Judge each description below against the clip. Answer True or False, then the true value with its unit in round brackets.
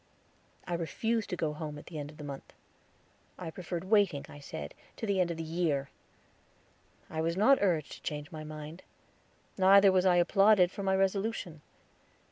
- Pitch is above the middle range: False (175 Hz)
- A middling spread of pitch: True (4.0 semitones)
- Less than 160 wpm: False (180 wpm)